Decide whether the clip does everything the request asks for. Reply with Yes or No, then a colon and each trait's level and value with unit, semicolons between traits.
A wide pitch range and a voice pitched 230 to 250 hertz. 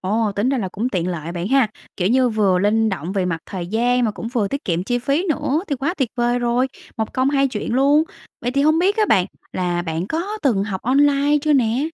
Yes: wide, 6.2 semitones; high, 240 Hz